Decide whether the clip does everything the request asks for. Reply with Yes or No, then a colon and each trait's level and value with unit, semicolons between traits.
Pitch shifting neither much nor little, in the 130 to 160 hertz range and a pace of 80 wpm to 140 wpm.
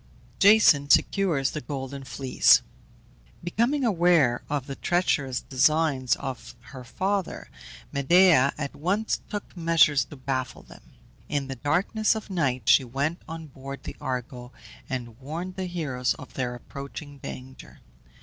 Yes: average, 5.0 semitones; medium, 140 Hz; slow, 135 wpm